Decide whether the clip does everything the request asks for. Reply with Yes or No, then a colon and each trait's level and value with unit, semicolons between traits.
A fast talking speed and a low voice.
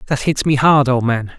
Yes: fast, 260 wpm; low, 130 Hz